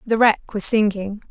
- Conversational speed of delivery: Yes, average, 185 wpm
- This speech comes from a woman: Yes, female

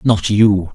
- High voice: No, low, 105 Hz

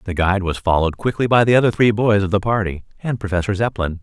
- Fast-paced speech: Yes, fast, 240 wpm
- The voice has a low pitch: Yes, low, 100 Hz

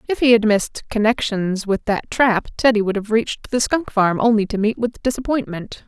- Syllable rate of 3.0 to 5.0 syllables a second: No, 5.2 syllables/s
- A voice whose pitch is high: Yes, high, 220 Hz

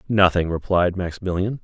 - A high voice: No, very low, 90 Hz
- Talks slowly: Yes, slow, 110 wpm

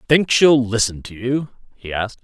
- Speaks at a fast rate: No, average, 190 wpm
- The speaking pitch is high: No, low, 120 Hz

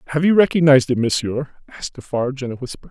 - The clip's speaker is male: Yes, male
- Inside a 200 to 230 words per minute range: Yes, fast, 205 wpm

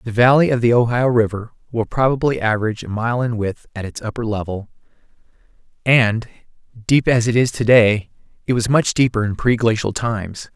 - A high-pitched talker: No, low, 115 Hz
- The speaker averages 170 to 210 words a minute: Yes, average, 175 wpm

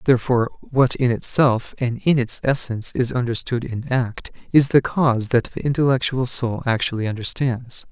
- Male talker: Yes, male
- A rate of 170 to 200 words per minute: No, average, 160 wpm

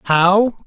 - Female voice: No, male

